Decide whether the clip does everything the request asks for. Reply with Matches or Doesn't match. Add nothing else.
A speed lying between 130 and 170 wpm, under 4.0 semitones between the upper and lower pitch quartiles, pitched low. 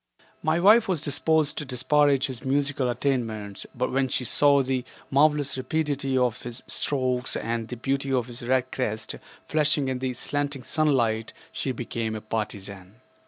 Matches